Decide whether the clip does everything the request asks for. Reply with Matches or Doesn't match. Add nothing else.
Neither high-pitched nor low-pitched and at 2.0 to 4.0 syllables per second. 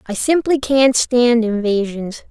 Doesn't match